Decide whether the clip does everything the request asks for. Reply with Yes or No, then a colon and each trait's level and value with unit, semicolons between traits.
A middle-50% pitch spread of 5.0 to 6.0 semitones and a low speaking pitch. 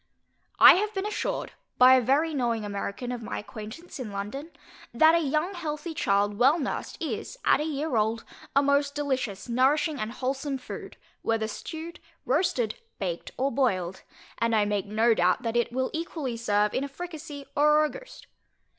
No: wide, 5.6 semitones; very high, 260 Hz